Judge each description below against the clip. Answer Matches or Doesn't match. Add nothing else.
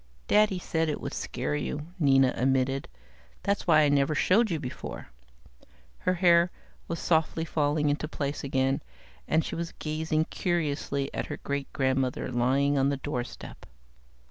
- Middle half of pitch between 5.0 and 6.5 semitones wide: Doesn't match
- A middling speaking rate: Matches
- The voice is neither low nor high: Matches